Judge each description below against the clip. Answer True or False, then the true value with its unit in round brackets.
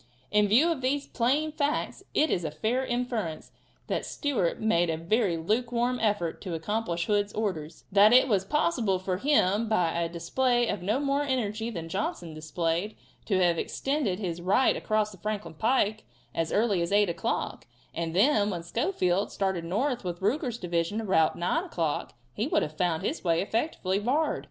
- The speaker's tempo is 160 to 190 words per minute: True (175 wpm)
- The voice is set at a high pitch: True (205 Hz)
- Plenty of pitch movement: True (5.9 semitones)